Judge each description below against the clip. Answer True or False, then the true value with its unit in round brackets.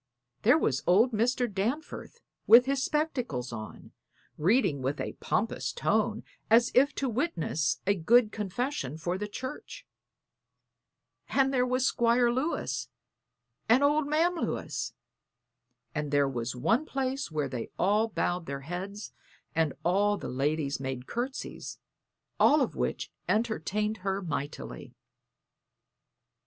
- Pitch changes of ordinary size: False (8.3 semitones)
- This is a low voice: False (210 Hz)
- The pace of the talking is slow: True (125 wpm)